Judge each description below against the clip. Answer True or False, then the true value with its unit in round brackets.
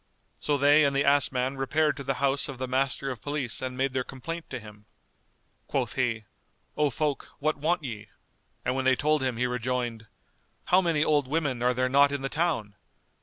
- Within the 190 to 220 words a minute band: True (205 wpm)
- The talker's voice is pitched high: False (135 Hz)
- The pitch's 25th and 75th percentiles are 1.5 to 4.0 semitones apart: True (2.6 semitones)